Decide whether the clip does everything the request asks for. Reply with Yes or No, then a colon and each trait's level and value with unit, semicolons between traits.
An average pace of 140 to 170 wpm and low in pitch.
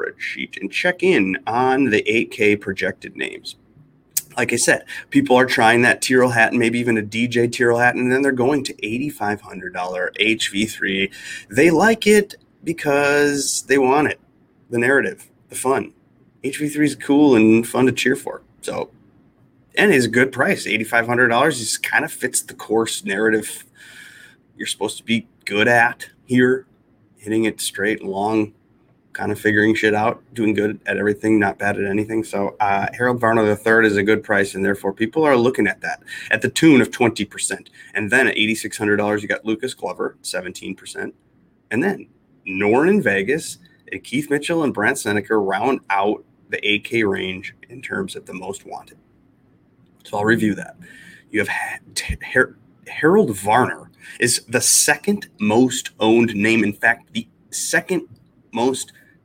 Yes: average, 165 wpm; low, 115 Hz